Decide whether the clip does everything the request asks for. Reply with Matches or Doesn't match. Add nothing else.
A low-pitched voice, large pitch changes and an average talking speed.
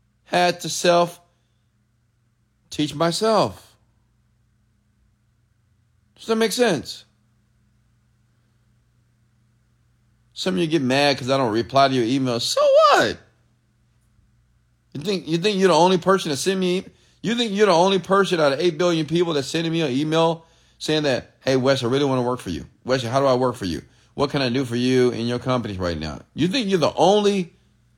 Matches